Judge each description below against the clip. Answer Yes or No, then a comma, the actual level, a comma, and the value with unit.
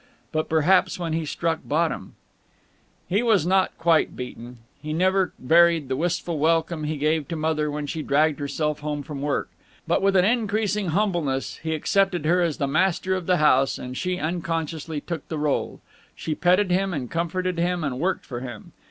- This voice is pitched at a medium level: Yes, medium, 160 Hz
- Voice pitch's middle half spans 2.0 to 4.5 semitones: Yes, average, 3.3 semitones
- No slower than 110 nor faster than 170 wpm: No, average, 185 wpm